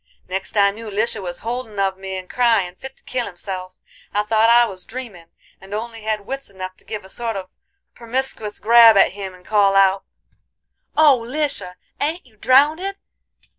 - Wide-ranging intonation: No, average, 3.9 semitones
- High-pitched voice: Yes, high, 215 Hz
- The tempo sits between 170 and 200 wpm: Yes, average, 180 wpm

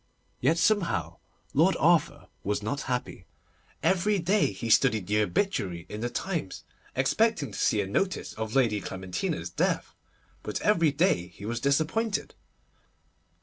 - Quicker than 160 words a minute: No, average, 145 wpm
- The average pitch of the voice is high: No, low, 125 Hz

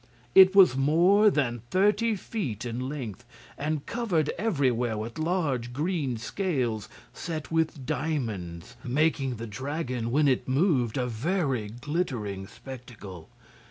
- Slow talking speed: Yes, slow, 125 wpm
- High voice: No, low, 135 Hz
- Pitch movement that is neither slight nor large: No, wide, 5.7 semitones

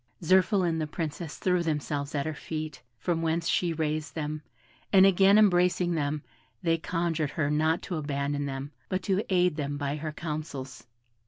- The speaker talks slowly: No, average, 170 wpm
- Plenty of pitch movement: No, average, 3.0 semitones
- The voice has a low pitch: No, medium, 160 Hz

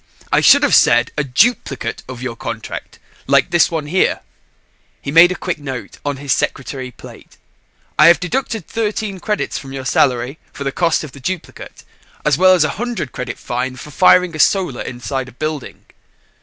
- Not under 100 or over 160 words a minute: No, average, 185 wpm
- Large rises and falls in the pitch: Yes, wide, 5.9 semitones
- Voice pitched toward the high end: No, medium, 145 Hz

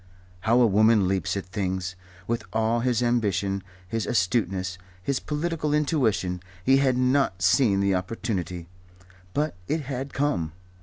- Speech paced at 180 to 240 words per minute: No, average, 140 wpm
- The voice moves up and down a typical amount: No, wide, 5.9 semitones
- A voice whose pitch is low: Yes, low, 110 Hz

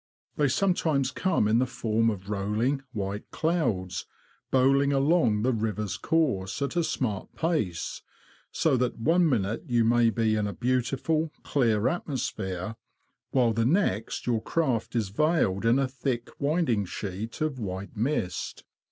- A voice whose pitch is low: Yes, low, 120 Hz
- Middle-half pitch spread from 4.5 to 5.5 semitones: Yes, average, 5.1 semitones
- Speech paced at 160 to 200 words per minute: No, average, 145 wpm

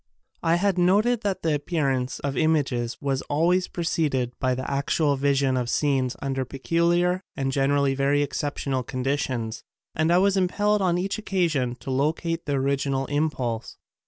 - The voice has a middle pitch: Yes, medium, 145 Hz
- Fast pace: No, average, 155 wpm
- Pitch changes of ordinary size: Yes, average, 4.4 semitones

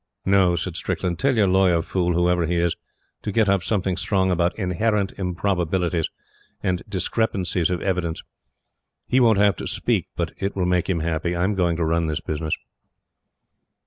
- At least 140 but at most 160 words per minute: No, average, 170 wpm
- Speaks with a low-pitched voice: Yes, very low, 90 Hz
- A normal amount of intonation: No, narrow, 2.3 semitones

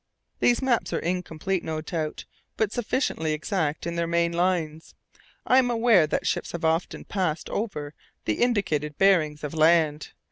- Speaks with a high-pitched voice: No, medium, 170 Hz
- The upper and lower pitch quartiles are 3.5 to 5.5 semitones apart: Yes, average, 4.1 semitones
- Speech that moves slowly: No, average, 155 wpm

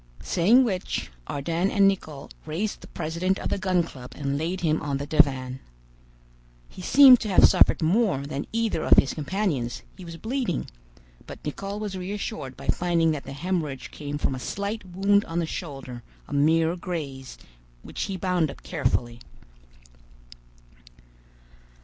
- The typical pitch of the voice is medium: Yes, medium, 165 Hz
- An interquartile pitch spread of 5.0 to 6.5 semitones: Yes, average, 5.3 semitones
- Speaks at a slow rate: No, average, 155 wpm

